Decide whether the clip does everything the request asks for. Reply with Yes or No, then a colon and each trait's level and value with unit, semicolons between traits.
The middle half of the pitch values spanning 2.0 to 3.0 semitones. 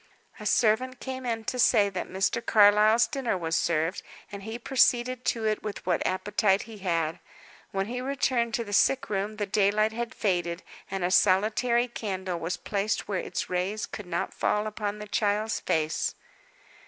No: average, 3.4 semitones